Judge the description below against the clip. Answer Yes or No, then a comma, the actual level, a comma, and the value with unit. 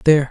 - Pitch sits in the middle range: Yes, medium, 145 Hz